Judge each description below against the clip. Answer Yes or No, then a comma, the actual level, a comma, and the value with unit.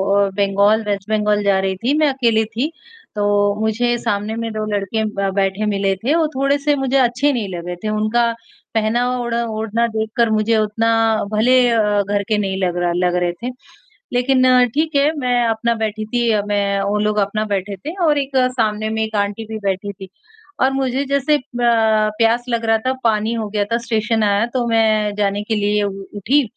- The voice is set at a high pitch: Yes, high, 220 Hz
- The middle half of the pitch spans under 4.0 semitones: Yes, average, 2.8 semitones